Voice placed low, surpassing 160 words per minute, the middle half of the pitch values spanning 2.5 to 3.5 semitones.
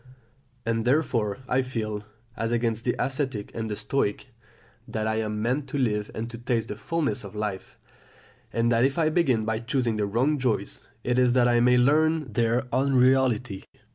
Yes: low, 120 Hz; average, 180 wpm; average, 3.1 semitones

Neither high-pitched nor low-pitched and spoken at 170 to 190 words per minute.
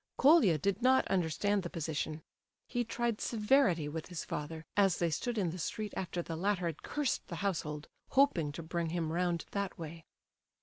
Yes: medium, 175 Hz; average, 180 wpm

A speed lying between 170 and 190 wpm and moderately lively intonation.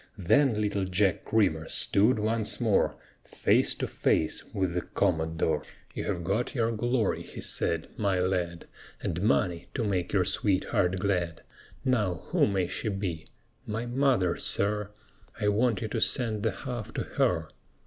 No: average, 155 wpm; average, 3.8 semitones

